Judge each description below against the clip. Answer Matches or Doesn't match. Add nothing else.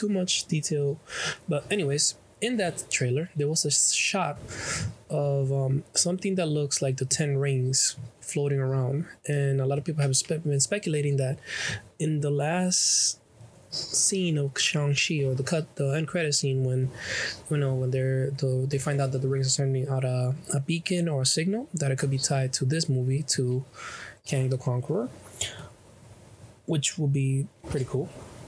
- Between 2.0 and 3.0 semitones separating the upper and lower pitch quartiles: Matches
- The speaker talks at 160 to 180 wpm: Matches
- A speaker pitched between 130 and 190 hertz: Matches